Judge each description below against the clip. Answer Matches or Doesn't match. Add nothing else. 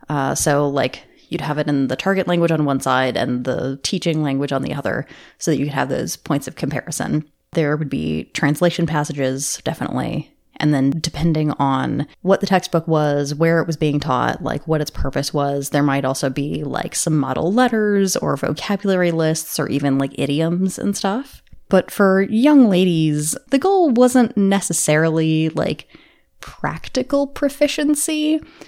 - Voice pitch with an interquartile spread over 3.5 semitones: Matches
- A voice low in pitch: Doesn't match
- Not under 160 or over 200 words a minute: Matches